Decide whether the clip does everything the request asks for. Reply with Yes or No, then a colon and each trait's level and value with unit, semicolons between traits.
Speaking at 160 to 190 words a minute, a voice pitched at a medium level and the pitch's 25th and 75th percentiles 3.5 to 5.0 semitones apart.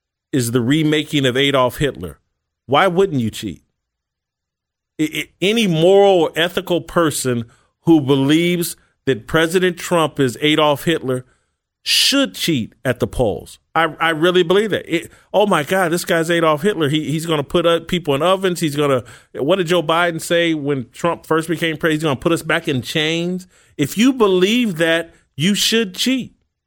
Yes: average, 180 wpm; medium, 160 Hz; average, 4.1 semitones